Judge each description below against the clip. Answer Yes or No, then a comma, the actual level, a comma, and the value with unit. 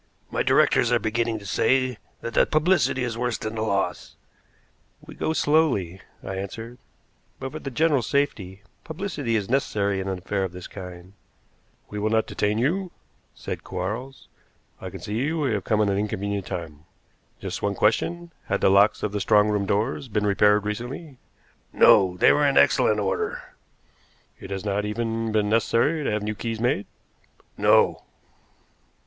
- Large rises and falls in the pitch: No, average, 4.4 semitones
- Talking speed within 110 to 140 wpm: No, average, 170 wpm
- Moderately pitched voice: No, low, 110 Hz